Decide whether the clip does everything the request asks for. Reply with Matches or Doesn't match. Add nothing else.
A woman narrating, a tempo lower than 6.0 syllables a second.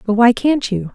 Matches